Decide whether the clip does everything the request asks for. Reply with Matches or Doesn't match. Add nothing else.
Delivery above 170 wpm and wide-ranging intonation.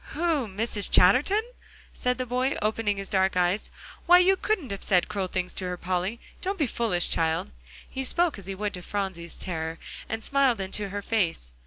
Matches